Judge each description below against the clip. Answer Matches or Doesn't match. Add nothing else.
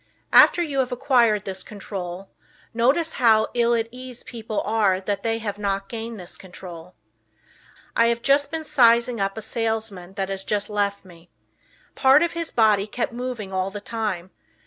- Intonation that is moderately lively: Matches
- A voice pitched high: Matches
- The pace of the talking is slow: Doesn't match